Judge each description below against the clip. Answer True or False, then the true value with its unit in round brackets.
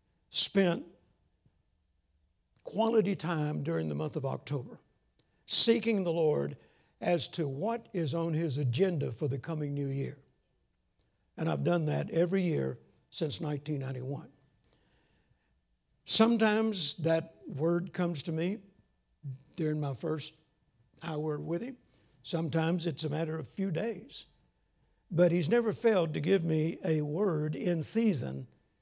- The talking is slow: True (130 wpm)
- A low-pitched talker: False (160 Hz)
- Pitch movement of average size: True (3.5 semitones)